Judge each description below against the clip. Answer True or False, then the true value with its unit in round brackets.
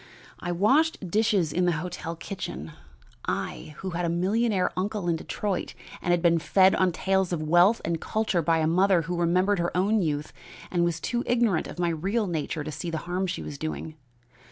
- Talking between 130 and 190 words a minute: False (200 wpm)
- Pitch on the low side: False (175 Hz)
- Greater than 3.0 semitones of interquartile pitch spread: False (2.7 semitones)